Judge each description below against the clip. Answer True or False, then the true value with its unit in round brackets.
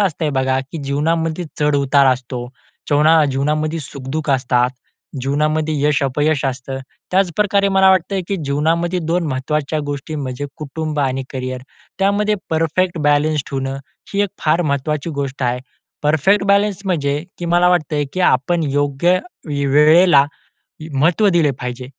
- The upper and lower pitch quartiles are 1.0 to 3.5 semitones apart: False (3.9 semitones)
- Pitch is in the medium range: True (150 Hz)